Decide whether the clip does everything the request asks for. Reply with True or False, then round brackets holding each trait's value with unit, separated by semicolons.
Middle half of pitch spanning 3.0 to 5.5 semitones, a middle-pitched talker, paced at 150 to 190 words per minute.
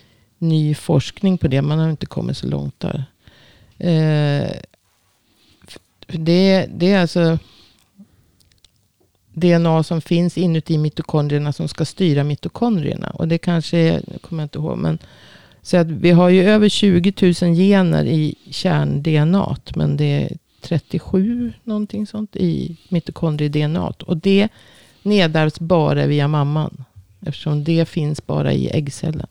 False (3.3 semitones; 165 Hz; 135 wpm)